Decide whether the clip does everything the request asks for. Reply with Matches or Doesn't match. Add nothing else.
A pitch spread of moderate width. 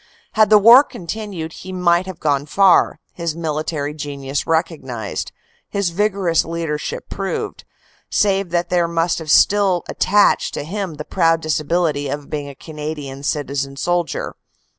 Matches